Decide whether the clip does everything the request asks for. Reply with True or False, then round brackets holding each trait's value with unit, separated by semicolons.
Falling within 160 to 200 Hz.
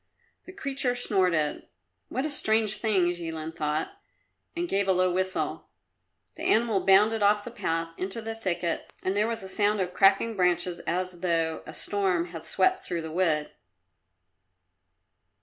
True (190 Hz)